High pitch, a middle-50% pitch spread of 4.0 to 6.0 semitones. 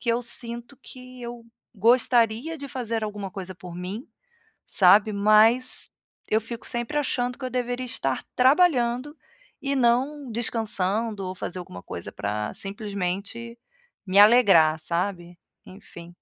Yes: high, 225 Hz; average, 4.5 semitones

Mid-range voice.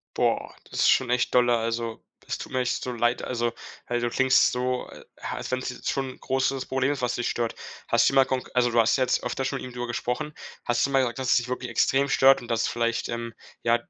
No: low, 125 Hz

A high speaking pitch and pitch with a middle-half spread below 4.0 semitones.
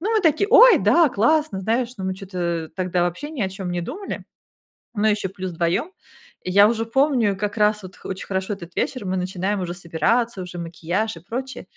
No: high, 200 Hz; average, 4.7 semitones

